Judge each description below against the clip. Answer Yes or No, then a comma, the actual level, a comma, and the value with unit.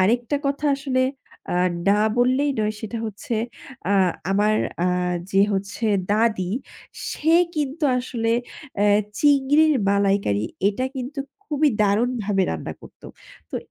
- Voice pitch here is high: Yes, high, 230 Hz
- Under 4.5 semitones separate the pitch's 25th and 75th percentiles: No, wide, 5.4 semitones